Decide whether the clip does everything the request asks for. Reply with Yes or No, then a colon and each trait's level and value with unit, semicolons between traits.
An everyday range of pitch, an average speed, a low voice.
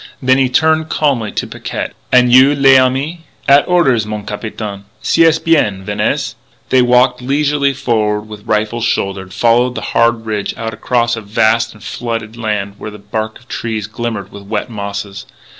Yes: average, 3.6 semitones; average, 165 wpm; low, 115 Hz